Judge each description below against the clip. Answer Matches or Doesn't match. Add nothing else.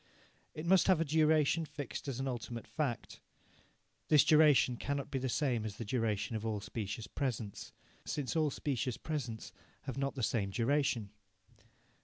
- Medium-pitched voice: Doesn't match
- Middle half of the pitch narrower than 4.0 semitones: Doesn't match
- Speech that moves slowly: Doesn't match